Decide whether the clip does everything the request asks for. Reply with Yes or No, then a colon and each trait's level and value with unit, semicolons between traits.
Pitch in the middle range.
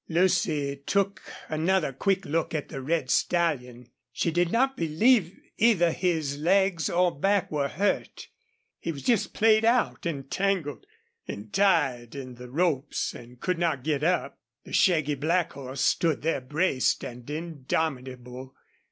Yes: medium, 160 Hz